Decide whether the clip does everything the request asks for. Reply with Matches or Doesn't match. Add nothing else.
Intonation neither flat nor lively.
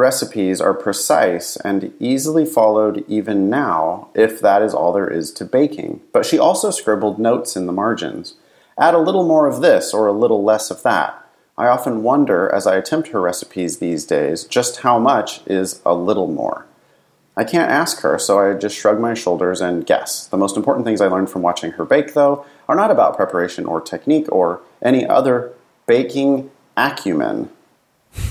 Doesn't match